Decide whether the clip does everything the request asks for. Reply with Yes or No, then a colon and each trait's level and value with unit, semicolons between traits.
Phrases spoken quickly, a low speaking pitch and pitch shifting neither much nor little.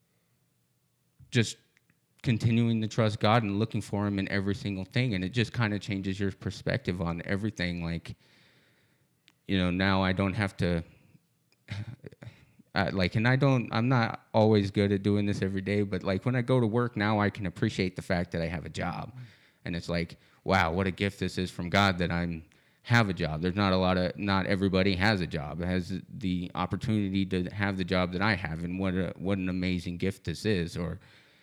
Yes: fast, 210 wpm; very low, 95 Hz; average, 3.1 semitones